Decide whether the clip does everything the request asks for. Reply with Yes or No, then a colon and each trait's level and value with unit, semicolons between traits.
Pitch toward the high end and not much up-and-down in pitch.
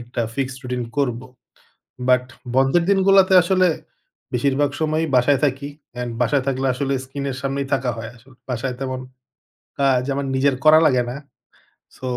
No: low, 135 Hz; narrow, 2.0 semitones